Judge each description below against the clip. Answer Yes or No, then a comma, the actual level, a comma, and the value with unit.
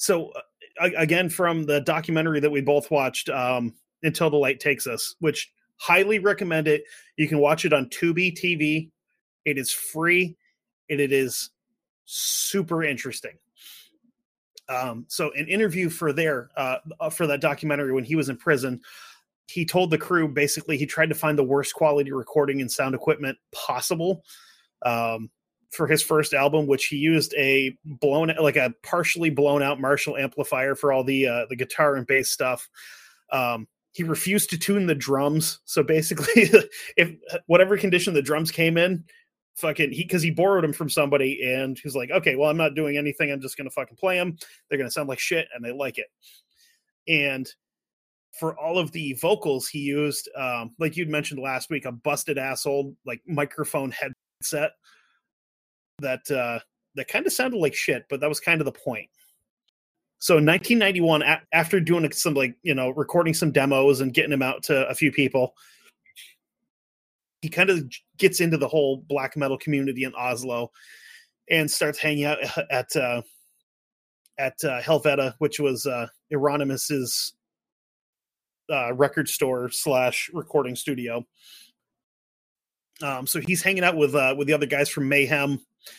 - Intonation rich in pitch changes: No, average, 3.6 semitones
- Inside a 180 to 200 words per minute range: No, average, 170 wpm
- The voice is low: No, medium, 150 Hz